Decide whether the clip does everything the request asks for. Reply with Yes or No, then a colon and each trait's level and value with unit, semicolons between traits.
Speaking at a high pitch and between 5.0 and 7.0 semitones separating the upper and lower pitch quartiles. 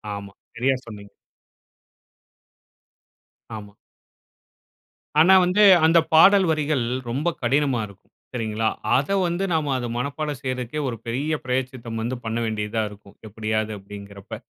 No: low, 125 Hz; average, 5.3 semitones